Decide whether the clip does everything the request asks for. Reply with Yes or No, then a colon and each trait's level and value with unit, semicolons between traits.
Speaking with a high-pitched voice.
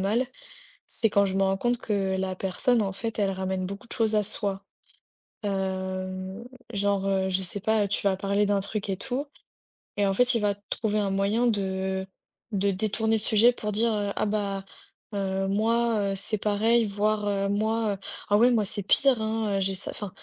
Yes: high, 200 Hz